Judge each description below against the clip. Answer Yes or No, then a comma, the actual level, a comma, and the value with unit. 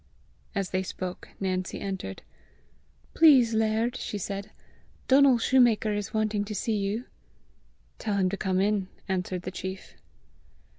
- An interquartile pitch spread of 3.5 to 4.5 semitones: No, average, 2.9 semitones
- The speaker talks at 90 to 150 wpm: Yes, slow, 135 wpm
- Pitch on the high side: Yes, high, 205 Hz